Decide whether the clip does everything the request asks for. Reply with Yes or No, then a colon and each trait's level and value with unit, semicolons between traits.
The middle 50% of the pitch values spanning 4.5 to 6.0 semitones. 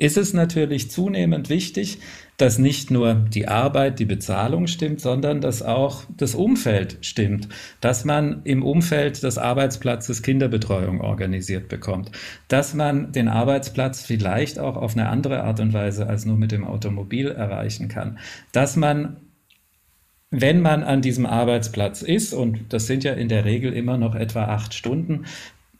Yes: average, 4.9 semitones